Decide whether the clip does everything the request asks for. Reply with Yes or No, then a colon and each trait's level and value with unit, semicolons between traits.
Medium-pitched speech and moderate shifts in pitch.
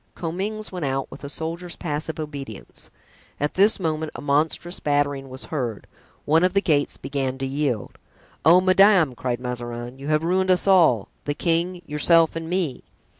Yes: medium, 155 Hz; average, 4.5 semitones